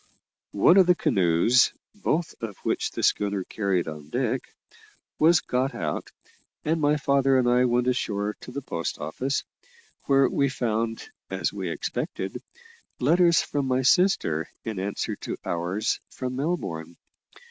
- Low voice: Yes, low, 125 Hz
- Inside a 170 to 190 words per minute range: No, average, 145 wpm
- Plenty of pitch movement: Yes, wide, 5.9 semitones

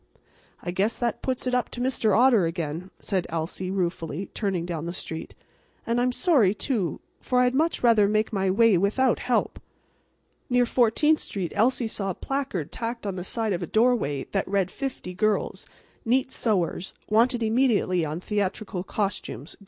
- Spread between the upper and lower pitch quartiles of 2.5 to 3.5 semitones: No, average, 5.0 semitones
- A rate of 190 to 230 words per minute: No, average, 170 wpm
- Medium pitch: No, high, 210 Hz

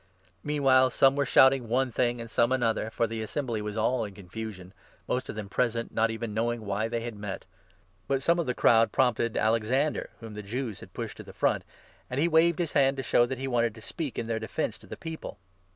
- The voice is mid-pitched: No, low, 120 Hz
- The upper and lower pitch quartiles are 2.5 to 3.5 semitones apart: Yes, average, 3.2 semitones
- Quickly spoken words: Yes, fast, 240 wpm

